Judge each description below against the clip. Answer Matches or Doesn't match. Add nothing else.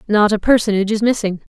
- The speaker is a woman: Matches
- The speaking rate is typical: Matches